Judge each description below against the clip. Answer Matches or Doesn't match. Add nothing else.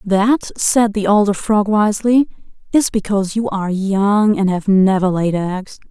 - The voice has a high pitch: Matches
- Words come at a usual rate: Matches